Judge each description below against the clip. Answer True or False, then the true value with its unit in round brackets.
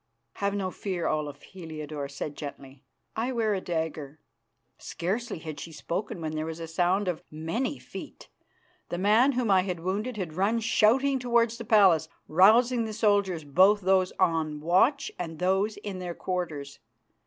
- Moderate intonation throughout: True (5.0 semitones)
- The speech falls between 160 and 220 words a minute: True (165 wpm)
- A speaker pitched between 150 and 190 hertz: True (185 Hz)